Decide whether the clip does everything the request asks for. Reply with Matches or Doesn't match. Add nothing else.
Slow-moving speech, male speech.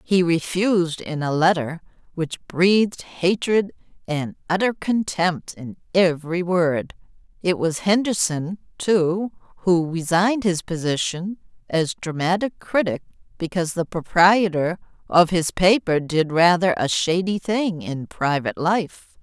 Doesn't match